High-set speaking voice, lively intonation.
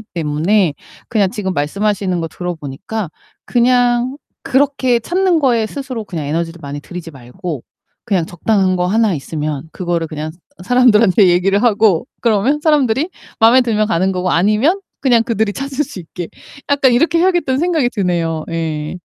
Yes: high, 205 Hz; wide, 6.5 semitones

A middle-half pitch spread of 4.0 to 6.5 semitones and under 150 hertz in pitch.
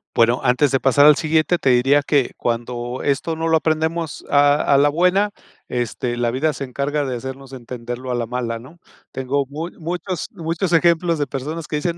Yes: average, 4.3 semitones; medium, 140 Hz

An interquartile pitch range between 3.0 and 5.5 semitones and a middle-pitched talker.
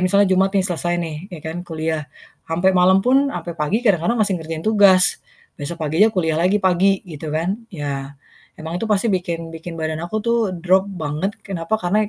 Yes: average, 3.5 semitones; medium, 180 Hz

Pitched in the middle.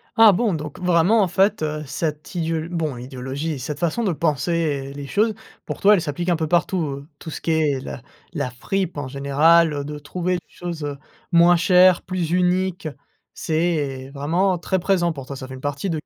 Yes: medium, 160 Hz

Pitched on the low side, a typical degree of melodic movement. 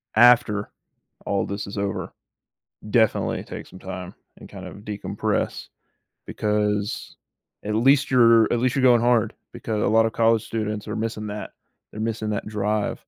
No: low, 110 Hz; narrow, 1.7 semitones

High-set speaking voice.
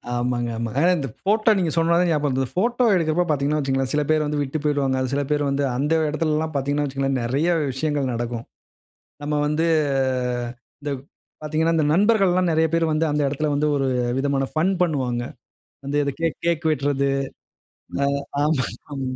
No: medium, 150 Hz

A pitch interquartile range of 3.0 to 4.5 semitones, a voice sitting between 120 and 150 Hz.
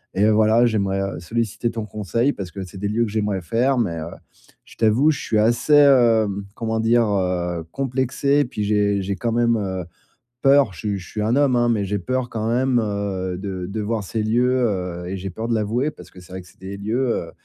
No: average, 3.4 semitones; low, 110 Hz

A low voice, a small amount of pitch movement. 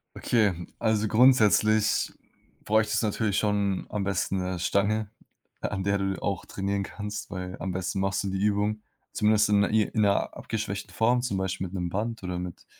Yes: low, 100 Hz; narrow, 2.0 semitones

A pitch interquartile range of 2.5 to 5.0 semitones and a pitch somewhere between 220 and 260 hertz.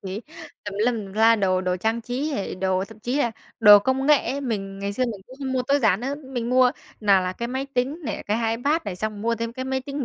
Yes: average, 4.4 semitones; high, 230 Hz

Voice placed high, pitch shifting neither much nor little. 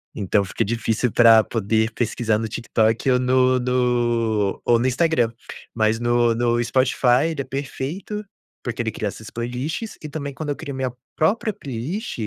No: low, 120 Hz; average, 3.0 semitones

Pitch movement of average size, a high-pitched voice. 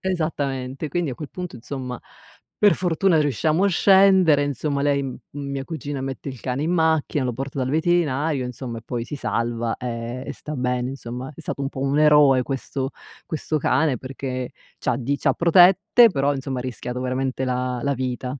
No: average, 3.5 semitones; low, 135 Hz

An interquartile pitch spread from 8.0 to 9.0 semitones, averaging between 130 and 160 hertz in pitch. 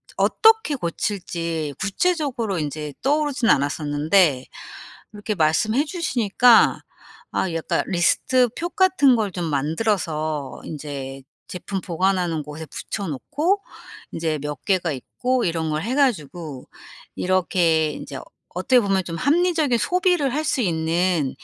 No: wide, 8.4 semitones; medium, 185 Hz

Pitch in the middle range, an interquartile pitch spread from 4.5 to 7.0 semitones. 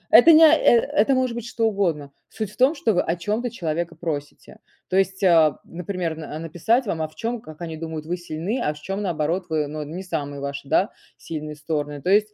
Yes: medium, 170 Hz; average, 5.3 semitones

